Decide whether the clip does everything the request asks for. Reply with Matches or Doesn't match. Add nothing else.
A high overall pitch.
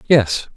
Doesn't match